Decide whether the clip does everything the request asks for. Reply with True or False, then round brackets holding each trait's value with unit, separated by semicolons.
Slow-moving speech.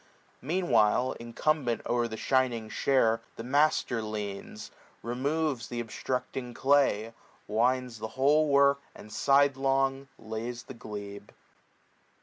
True (115 wpm)